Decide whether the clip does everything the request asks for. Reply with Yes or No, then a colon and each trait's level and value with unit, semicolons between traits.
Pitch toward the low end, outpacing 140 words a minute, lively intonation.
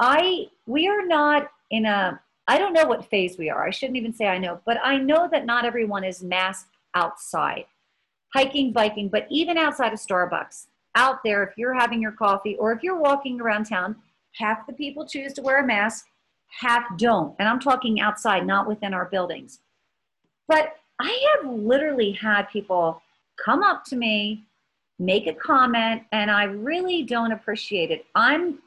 No: high, 230 Hz; average, 180 wpm; wide, 5.7 semitones